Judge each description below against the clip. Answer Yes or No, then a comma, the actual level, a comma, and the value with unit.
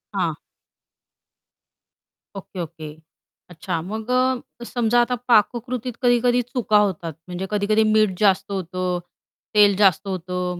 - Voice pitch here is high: Yes, high, 200 Hz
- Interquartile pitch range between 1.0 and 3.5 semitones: No, average, 3.9 semitones